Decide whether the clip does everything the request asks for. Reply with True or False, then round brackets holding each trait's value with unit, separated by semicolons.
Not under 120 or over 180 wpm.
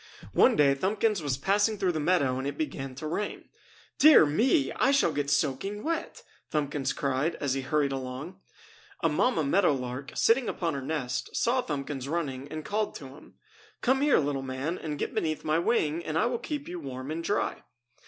False (195 wpm)